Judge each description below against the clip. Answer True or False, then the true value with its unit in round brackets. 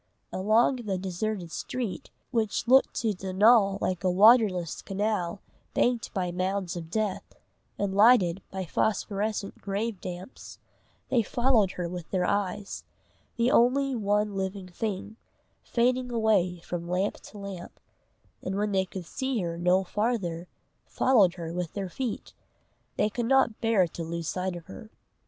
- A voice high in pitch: True (195 Hz)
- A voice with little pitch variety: False (3.4 semitones)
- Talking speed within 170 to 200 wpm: False (145 wpm)